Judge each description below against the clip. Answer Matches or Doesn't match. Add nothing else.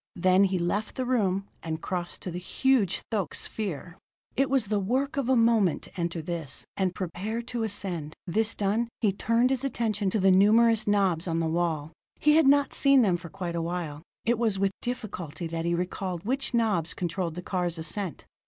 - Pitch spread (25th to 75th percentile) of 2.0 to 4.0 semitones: Doesn't match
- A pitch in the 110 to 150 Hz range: Doesn't match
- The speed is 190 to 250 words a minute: Matches